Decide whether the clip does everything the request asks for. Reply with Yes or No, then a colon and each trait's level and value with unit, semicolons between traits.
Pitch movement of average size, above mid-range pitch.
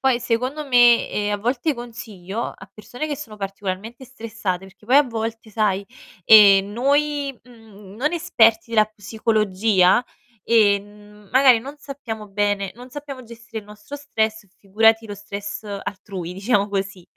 Yes: average, 3.2 semitones; high, 220 Hz